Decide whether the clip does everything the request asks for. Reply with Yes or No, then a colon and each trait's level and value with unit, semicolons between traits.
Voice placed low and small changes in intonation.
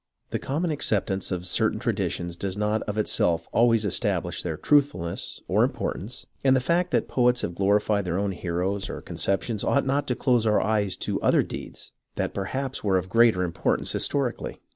No: low, 105 Hz; average, 5.1 semitones